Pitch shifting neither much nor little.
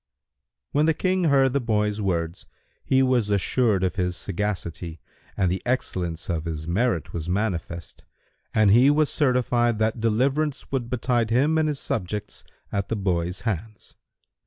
No: wide, 6.0 semitones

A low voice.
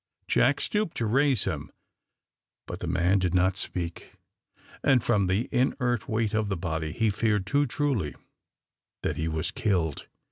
Yes: low, 100 Hz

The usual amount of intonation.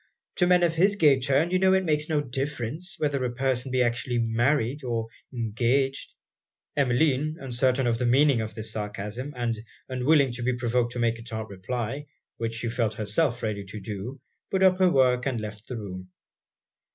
Yes: average, 4.0 semitones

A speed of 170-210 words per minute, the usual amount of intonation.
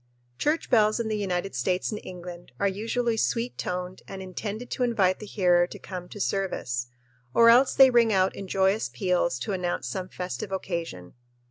Yes: average, 185 wpm; average, 3.5 semitones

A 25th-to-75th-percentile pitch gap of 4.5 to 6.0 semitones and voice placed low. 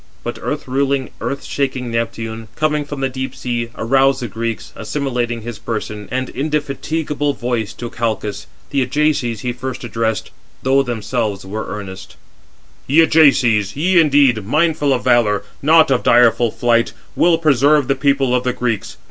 No: average, 3.5 semitones; low, 125 Hz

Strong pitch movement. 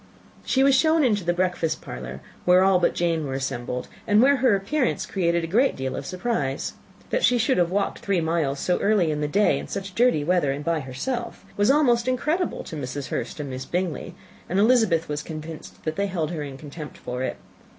Yes: wide, 6.8 semitones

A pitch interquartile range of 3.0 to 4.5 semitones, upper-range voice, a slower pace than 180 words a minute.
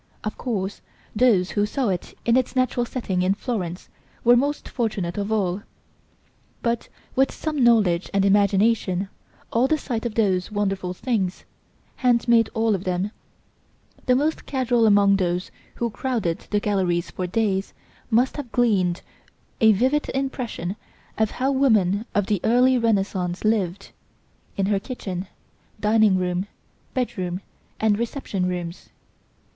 Yes: average, 4.2 semitones; high, 210 Hz; average, 140 wpm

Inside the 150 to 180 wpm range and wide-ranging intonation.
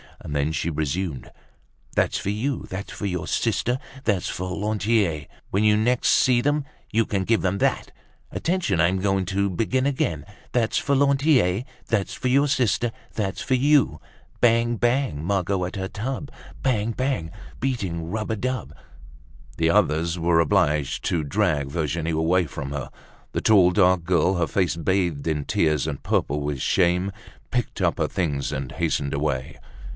Yes: average, 165 wpm; wide, 6.3 semitones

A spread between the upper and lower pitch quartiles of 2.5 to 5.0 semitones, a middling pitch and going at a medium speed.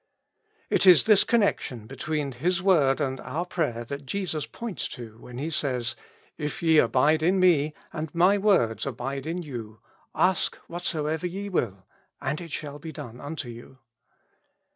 No: wide, 5.4 semitones; medium, 150 Hz; average, 165 wpm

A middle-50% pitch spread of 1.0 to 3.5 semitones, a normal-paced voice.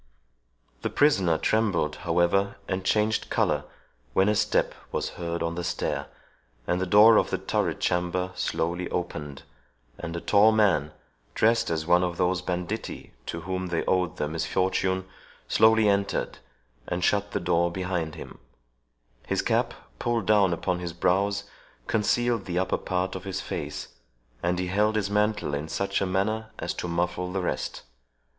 Yes: average, 2.8 semitones; average, 160 wpm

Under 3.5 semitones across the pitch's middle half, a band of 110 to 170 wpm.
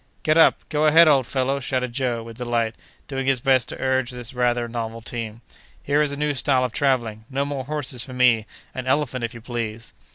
No: average, 2.7 semitones; average, 200 wpm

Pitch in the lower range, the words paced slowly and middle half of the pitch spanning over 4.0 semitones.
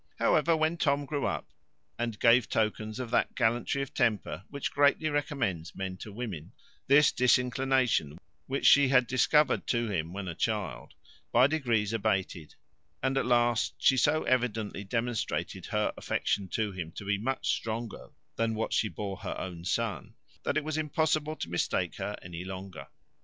No: low, 115 Hz; average, 165 wpm; average, 5.2 semitones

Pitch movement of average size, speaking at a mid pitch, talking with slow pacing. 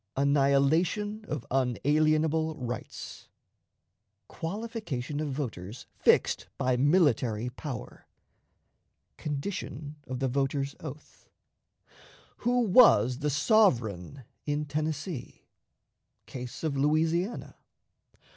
Yes: average, 3.7 semitones; medium, 145 Hz; slow, 80 wpm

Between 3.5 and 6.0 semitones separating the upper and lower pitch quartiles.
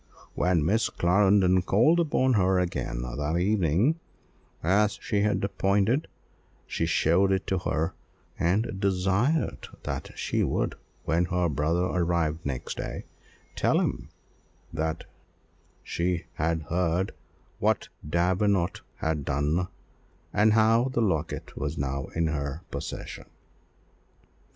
Yes: average, 4.0 semitones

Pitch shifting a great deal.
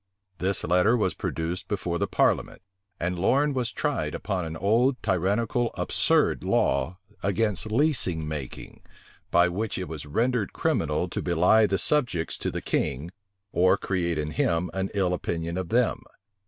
No: average, 4.5 semitones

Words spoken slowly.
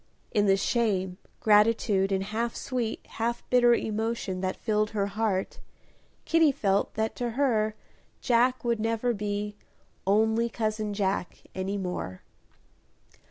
Yes: slow, 125 wpm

